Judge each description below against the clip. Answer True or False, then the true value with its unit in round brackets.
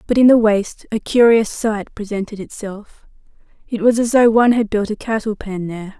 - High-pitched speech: True (215 Hz)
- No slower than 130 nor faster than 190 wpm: False (200 wpm)